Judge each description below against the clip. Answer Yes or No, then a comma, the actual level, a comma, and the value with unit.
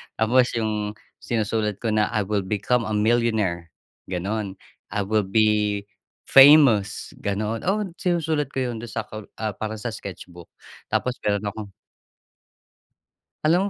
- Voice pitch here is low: Yes, low, 110 Hz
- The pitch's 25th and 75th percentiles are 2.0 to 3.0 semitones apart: Yes, average, 2.7 semitones